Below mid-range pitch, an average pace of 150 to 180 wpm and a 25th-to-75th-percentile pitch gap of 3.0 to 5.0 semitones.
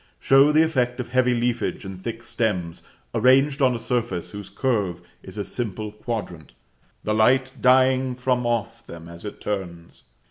Yes: low, 120 Hz; average, 165 wpm; average, 4.2 semitones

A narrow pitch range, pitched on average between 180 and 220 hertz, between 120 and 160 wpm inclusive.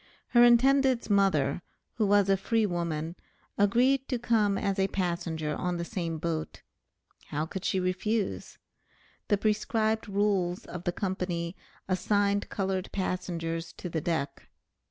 No: average, 3.6 semitones; high, 190 Hz; slow, 135 wpm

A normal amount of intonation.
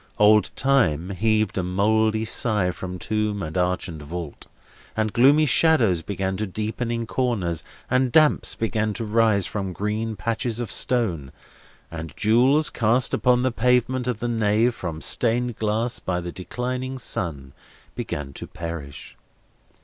Yes: average, 4.8 semitones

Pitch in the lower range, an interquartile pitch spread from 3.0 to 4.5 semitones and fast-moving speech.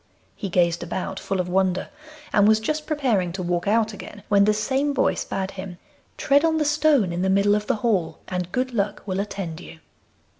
No: high, 200 Hz; average, 4.2 semitones; fast, 210 wpm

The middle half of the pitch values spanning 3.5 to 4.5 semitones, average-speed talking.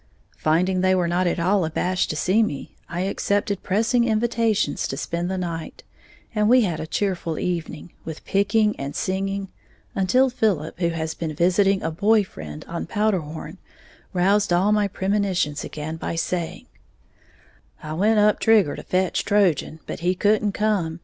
Yes: average, 3.8 semitones; average, 165 wpm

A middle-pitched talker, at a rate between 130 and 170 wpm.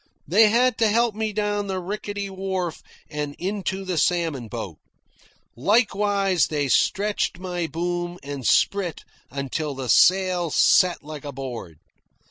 Yes: medium, 180 Hz; slow, 135 wpm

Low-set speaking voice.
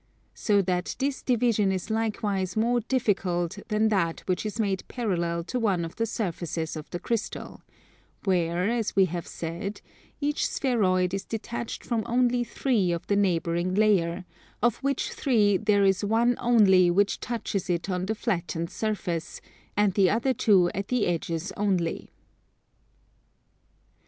No: high, 200 Hz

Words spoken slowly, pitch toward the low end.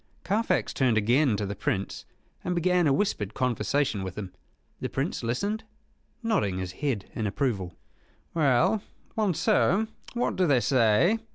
No: average, 145 wpm; low, 130 Hz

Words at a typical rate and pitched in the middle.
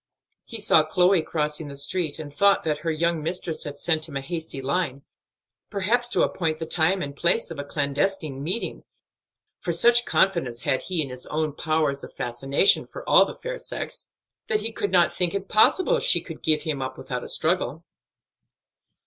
Yes: average, 190 wpm; medium, 160 Hz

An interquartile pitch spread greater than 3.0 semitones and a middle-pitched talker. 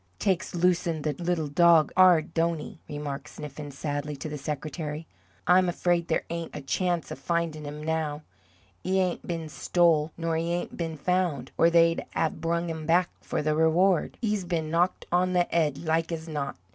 No: narrow, 2.4 semitones; medium, 165 Hz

